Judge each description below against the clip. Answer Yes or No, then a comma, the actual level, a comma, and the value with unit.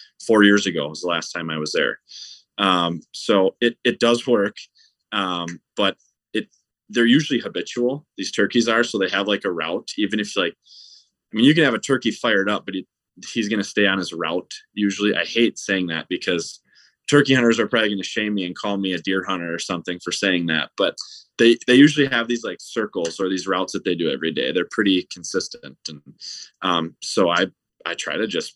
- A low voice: Yes, low, 100 Hz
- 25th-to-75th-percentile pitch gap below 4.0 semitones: No, average, 4.6 semitones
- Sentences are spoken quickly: Yes, fast, 220 wpm